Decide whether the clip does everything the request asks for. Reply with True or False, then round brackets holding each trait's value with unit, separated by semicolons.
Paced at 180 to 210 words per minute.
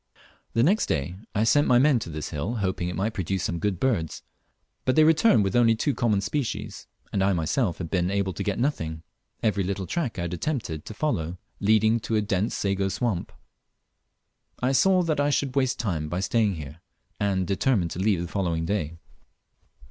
True (195 wpm)